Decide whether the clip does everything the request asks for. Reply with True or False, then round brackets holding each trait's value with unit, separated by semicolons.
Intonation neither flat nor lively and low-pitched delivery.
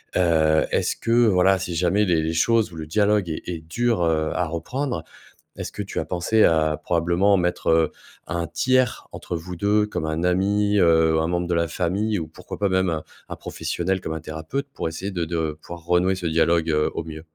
True (3.2 semitones; 85 Hz)